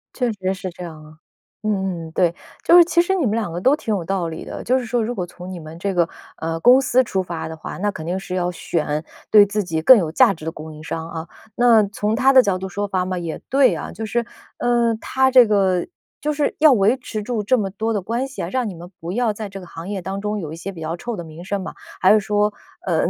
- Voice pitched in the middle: No, high, 195 Hz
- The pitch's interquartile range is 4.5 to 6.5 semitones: Yes, average, 5.0 semitones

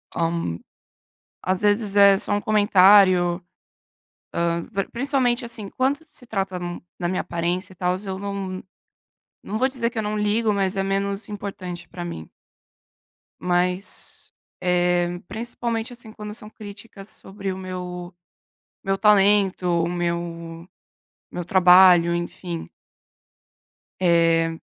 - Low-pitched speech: No, high, 190 Hz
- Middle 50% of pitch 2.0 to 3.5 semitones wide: Yes, average, 3.0 semitones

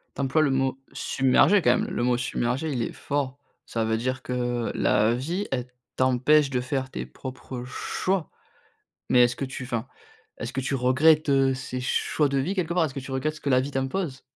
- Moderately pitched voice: No, low, 130 Hz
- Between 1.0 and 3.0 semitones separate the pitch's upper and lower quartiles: Yes, narrow, 2.5 semitones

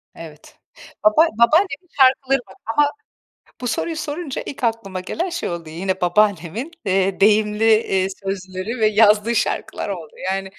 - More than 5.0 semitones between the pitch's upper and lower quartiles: Yes, wide, 5.5 semitones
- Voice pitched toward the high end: Yes, high, 210 Hz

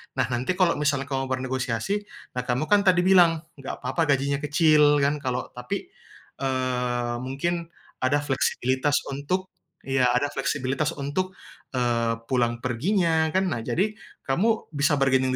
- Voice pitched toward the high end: No, medium, 140 Hz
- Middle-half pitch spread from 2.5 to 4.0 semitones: No, average, 4.4 semitones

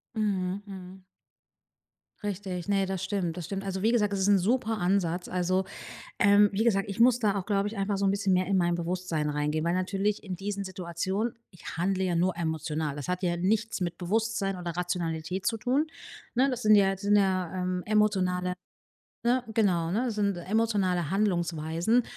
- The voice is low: No, high, 190 Hz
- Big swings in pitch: No, average, 2.7 semitones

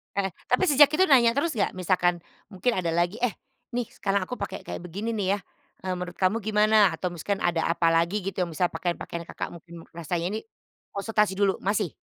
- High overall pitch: Yes, high, 195 Hz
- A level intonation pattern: No, average, 3.7 semitones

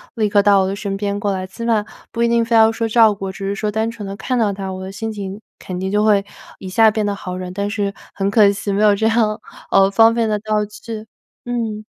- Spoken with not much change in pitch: Yes, narrow, 2.0 semitones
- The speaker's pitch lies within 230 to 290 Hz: No, high, 205 Hz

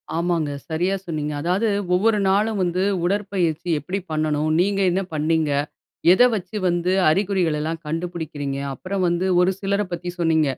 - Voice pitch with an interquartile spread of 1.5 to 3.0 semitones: No, average, 3.4 semitones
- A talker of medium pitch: Yes, medium, 175 Hz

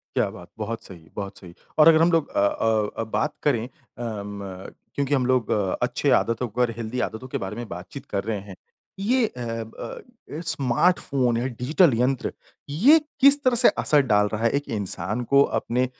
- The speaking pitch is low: Yes, low, 120 Hz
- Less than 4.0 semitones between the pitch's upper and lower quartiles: No, average, 5.0 semitones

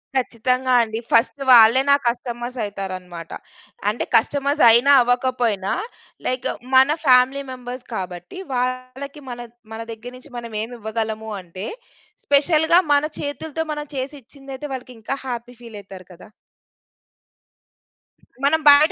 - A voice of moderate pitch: No, high, 245 Hz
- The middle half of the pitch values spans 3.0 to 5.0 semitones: Yes, average, 3.6 semitones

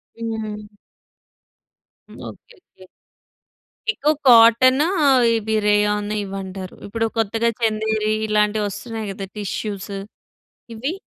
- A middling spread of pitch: No, narrow, 1.6 semitones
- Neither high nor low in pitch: No, high, 215 Hz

